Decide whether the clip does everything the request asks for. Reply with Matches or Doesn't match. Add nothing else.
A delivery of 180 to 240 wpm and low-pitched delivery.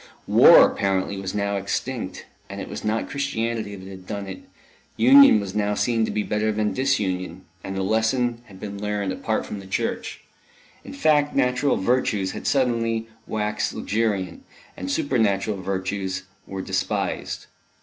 Doesn't match